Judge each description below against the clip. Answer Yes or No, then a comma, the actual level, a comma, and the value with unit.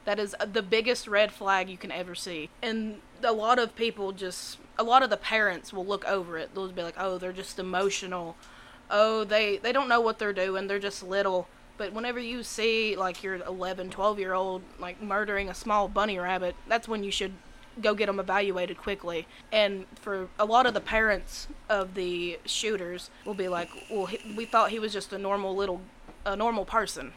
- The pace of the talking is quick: Yes, fast, 210 wpm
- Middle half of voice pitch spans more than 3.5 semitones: No, average, 2.8 semitones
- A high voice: Yes, high, 200 Hz